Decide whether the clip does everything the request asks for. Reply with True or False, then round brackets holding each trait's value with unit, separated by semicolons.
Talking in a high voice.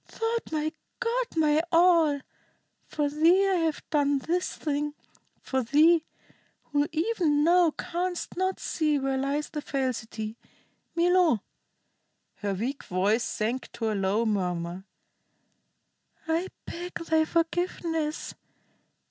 True (305 Hz)